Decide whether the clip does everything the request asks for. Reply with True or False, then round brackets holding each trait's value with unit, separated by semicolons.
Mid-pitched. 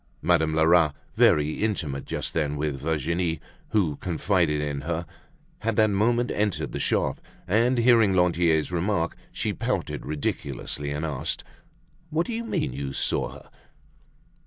False (85 Hz)